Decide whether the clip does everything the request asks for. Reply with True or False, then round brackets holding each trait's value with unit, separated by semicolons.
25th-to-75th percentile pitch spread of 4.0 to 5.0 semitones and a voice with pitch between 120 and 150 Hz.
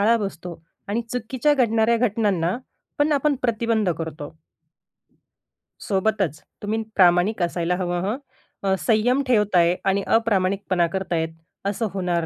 False (4.4 semitones; 200 Hz)